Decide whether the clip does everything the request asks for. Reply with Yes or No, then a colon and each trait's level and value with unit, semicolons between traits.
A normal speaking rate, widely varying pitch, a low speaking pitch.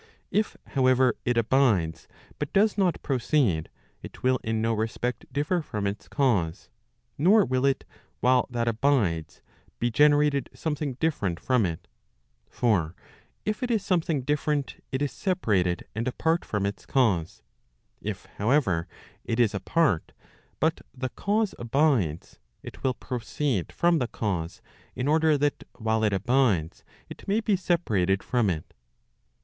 Yes: average, 145 wpm; wide, 6.3 semitones; low, 125 Hz